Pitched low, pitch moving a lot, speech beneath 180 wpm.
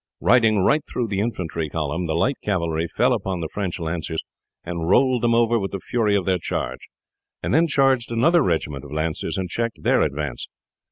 No: very low, 95 Hz; wide, 6.2 semitones; average, 190 wpm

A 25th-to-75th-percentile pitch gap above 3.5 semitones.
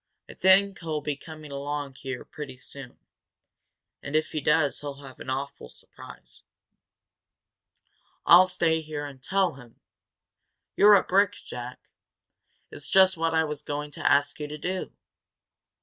No: average, 3.2 semitones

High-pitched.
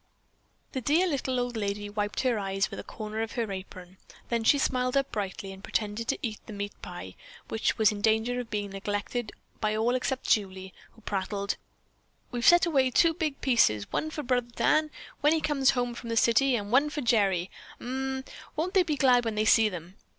Yes: high, 230 Hz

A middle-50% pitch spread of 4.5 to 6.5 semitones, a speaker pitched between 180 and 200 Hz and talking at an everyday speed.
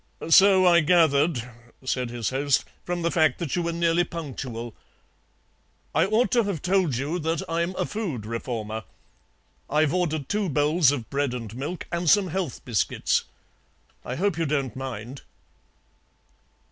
No: average, 5.1 semitones; medium, 155 Hz; average, 150 wpm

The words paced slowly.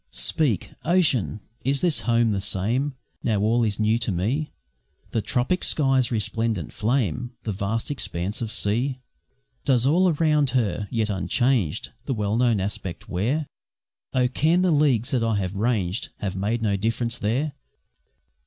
No: average, 155 wpm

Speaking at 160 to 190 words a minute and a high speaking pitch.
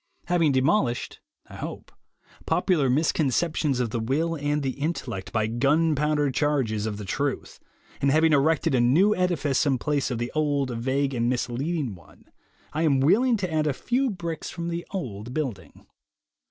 No: average, 165 wpm; medium, 145 Hz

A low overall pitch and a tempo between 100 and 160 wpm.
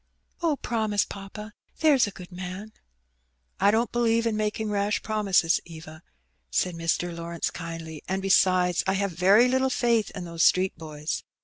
No: high, 195 Hz; average, 155 wpm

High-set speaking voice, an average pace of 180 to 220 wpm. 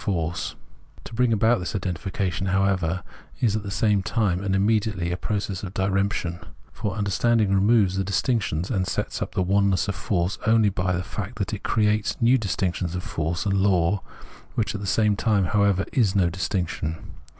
No: low, 100 Hz; average, 190 wpm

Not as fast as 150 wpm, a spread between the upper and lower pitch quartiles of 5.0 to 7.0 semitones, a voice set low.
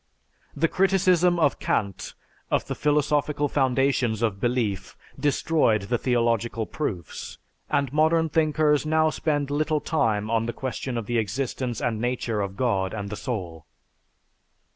Yes: average, 140 wpm; wide, 5.4 semitones; low, 125 Hz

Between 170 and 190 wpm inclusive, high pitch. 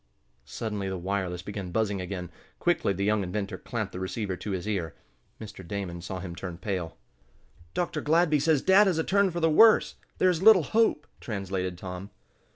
No: average, 180 wpm; low, 100 Hz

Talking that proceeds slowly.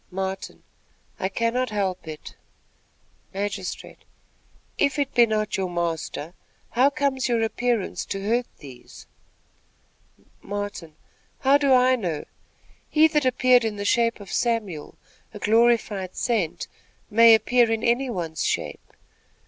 Yes: slow, 125 wpm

